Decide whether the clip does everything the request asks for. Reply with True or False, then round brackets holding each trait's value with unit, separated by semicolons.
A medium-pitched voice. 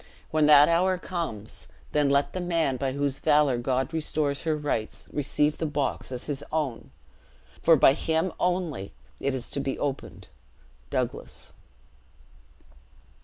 True (145 Hz)